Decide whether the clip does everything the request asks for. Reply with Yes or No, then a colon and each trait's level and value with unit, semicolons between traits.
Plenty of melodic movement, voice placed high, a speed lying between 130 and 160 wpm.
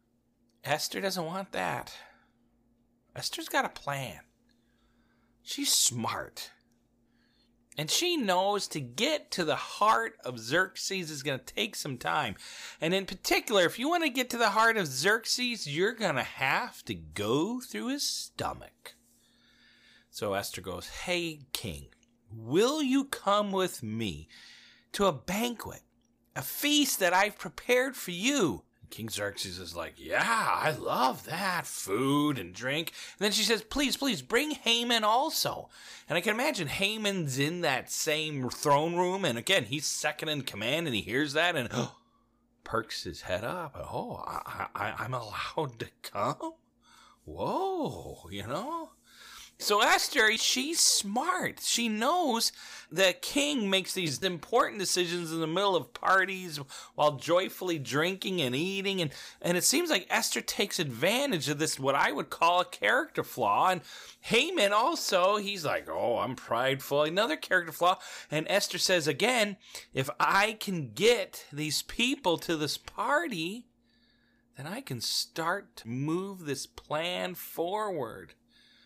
No: wide, 8.0 semitones; medium, 180 Hz; average, 150 wpm